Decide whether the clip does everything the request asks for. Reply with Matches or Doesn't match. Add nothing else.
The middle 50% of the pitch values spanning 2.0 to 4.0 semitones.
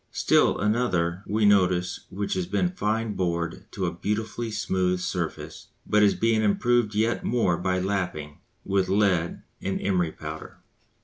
Matches